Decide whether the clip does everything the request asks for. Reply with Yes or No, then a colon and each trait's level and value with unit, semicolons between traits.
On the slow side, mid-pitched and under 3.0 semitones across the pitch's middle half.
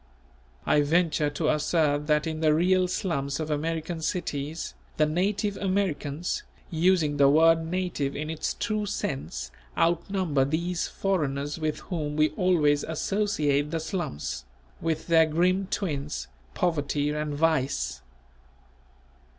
No: slow, 125 wpm; medium, 155 Hz; average, 3.3 semitones